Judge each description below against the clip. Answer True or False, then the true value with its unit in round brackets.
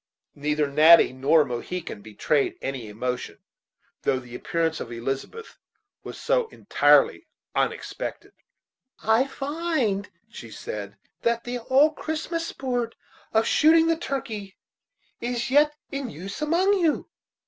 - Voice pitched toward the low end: False (225 Hz)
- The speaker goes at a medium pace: False (120 wpm)